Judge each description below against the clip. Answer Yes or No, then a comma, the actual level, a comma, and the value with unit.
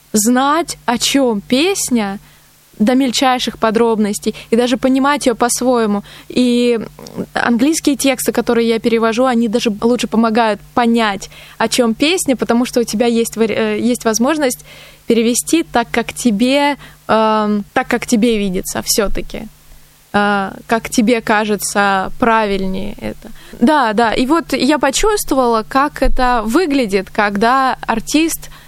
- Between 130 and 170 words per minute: No, average, 120 wpm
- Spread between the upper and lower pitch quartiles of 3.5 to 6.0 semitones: No, average, 2.9 semitones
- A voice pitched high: Yes, high, 235 Hz